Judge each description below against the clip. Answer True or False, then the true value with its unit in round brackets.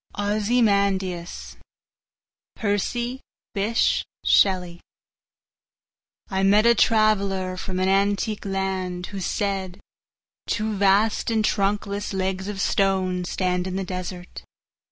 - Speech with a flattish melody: True (1.8 semitones)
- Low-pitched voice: False (195 Hz)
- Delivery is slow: True (90 wpm)